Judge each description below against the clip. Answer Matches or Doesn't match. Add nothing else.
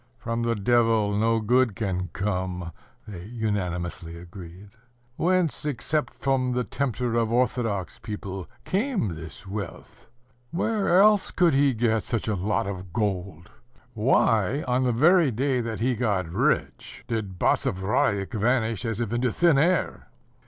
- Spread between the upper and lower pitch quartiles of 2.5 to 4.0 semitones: Doesn't match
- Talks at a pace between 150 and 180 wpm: Doesn't match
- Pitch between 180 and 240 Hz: Doesn't match